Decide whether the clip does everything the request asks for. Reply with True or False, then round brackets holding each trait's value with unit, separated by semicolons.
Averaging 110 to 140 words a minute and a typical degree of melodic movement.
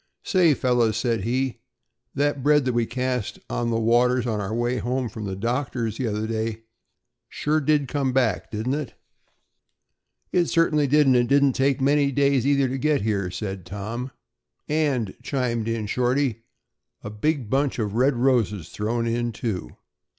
False (165 wpm; 3.8 semitones)